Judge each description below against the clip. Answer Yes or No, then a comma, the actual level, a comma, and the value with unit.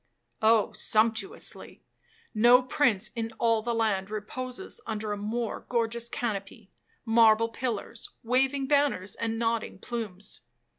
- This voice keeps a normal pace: No, slow, 110 wpm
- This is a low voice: No, high, 225 Hz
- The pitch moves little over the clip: Yes, narrow, 2.0 semitones